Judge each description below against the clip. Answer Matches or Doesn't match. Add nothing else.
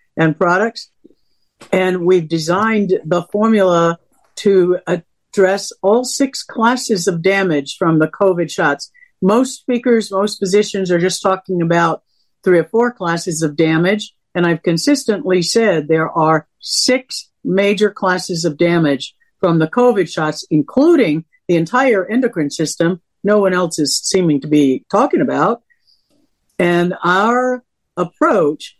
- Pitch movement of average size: Matches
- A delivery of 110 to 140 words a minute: Matches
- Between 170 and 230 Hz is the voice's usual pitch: Matches